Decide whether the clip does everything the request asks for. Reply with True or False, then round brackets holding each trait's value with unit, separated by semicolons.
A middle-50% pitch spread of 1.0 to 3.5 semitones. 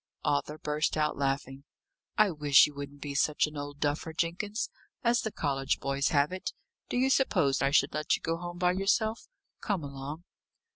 False (4.0 semitones)